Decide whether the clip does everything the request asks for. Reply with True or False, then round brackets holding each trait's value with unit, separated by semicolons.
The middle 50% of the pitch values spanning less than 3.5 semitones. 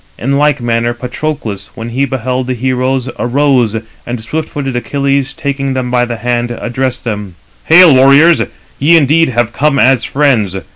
True (2.7 semitones)